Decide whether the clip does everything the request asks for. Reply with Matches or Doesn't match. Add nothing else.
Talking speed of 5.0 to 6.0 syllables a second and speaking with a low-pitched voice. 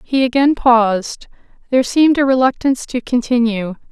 Doesn't match